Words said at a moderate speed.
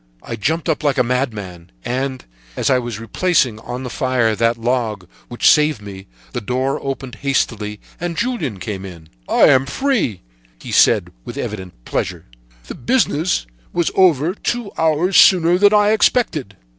Yes: average, 165 wpm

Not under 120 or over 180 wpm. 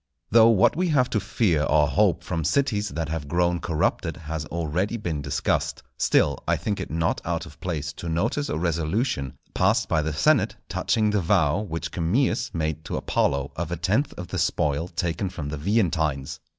No: average, 190 wpm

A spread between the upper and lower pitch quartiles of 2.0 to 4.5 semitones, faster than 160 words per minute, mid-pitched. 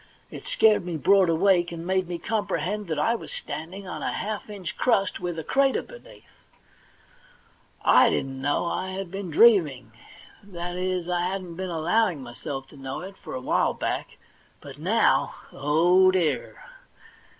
Yes: average, 3.4 semitones; average, 170 wpm; medium, 180 Hz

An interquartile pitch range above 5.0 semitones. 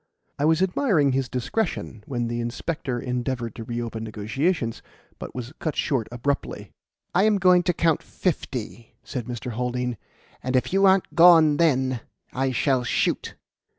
Yes: wide, 5.5 semitones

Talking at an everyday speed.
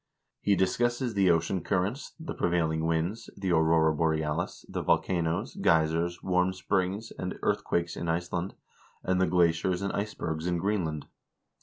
Yes: average, 145 wpm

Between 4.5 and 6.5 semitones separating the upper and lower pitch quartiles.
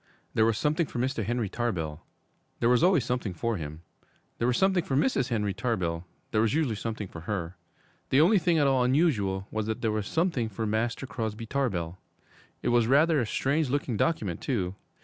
Yes: average, 5.0 semitones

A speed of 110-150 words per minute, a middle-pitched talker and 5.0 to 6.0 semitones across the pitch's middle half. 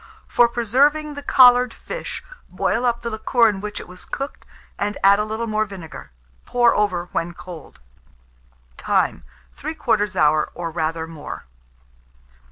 No: average, 145 wpm; high, 215 Hz; wide, 5.5 semitones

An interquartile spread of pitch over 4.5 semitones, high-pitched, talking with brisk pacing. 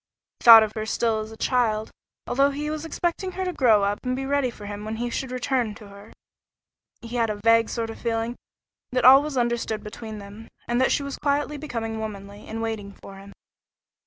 No: average, 3.4 semitones; high, 230 Hz; fast, 220 wpm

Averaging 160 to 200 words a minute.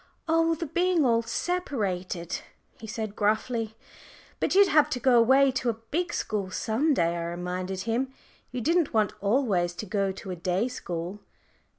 Yes: average, 175 wpm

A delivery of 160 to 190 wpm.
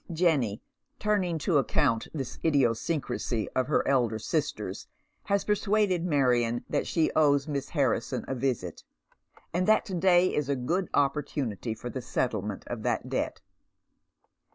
No: average, 140 wpm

